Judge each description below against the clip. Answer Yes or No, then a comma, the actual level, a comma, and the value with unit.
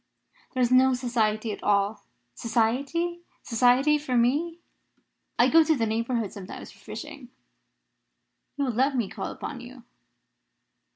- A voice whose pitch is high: Yes, very high, 250 Hz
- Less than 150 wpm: Yes, slow, 135 wpm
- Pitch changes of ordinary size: Yes, average, 3.7 semitones